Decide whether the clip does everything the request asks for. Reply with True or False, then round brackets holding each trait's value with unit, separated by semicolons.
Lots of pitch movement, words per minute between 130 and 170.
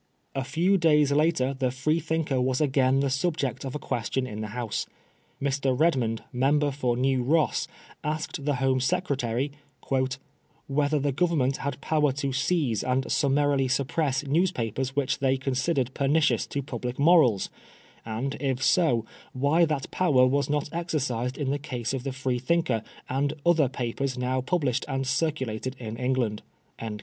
False (2.6 semitones; 150 wpm)